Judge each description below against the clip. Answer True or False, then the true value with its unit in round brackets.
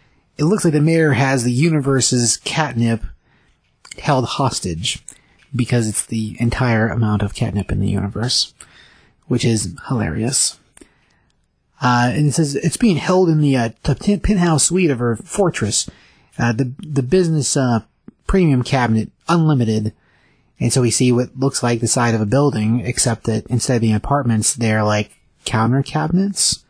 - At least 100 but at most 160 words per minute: True (155 wpm)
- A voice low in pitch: True (125 Hz)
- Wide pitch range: False (4.9 semitones)